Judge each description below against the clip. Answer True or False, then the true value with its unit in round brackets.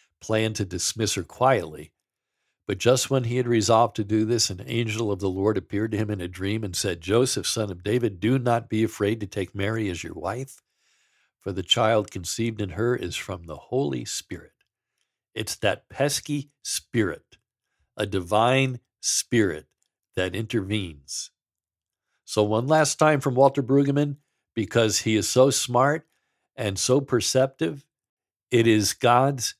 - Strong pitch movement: False (3.7 semitones)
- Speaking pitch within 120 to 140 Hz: False (110 Hz)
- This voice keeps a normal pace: True (160 wpm)